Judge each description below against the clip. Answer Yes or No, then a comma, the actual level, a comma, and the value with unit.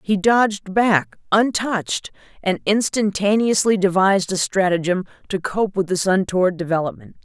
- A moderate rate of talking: No, slow, 125 wpm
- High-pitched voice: Yes, high, 195 Hz